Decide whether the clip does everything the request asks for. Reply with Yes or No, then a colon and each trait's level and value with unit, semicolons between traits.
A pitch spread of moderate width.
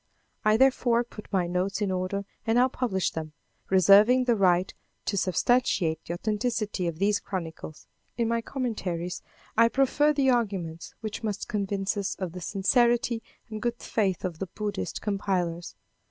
Yes: average, 4.2 semitones